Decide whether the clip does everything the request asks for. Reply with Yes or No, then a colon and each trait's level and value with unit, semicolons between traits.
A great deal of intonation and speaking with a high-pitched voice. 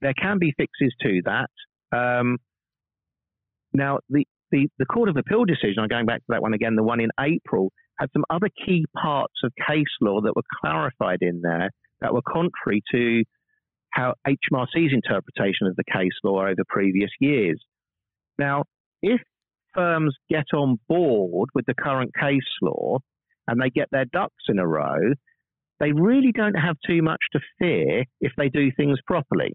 No: wide, 5.9 semitones; medium, 140 Hz